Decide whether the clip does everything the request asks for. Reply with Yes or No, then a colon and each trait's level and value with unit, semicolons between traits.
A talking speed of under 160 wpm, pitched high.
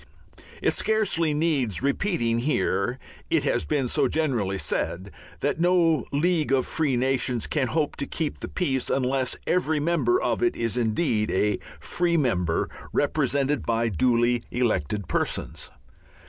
No: average, 140 wpm; low, 135 Hz